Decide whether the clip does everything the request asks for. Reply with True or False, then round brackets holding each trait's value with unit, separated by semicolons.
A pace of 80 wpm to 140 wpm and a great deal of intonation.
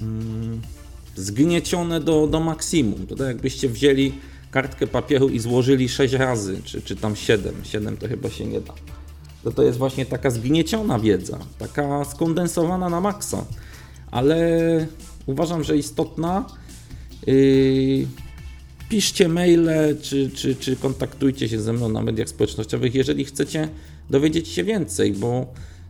True (130 wpm; 6.0 semitones)